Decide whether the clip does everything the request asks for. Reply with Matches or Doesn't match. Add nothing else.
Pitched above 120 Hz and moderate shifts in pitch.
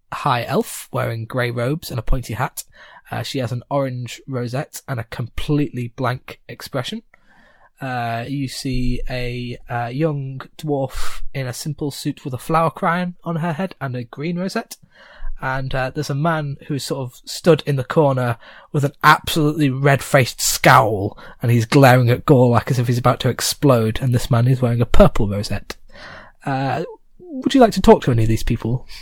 Matches